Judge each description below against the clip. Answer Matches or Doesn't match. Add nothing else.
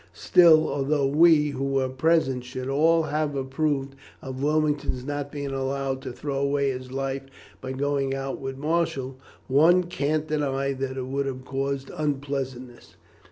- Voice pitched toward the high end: Doesn't match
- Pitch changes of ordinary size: Doesn't match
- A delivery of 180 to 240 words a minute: Doesn't match